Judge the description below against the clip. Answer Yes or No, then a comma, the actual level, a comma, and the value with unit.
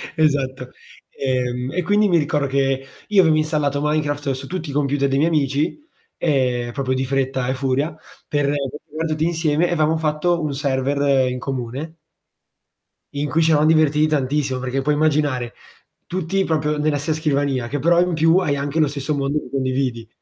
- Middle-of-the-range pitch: Yes, medium, 145 Hz